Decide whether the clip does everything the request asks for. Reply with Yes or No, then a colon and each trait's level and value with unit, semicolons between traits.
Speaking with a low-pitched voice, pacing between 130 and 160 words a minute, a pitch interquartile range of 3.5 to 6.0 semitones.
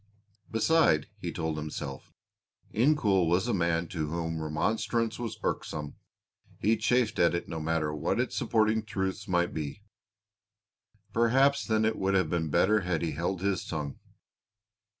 Yes: very low, 90 Hz; average, 150 wpm; wide, 5.4 semitones